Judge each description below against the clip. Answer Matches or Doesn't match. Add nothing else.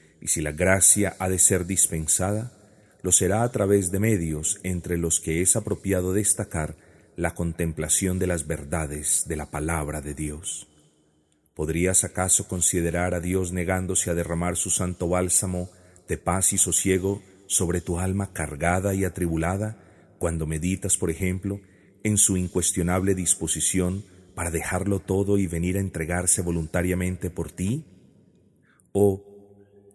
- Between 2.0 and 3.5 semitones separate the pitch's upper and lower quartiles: Matches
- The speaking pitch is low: Matches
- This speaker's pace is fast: Doesn't match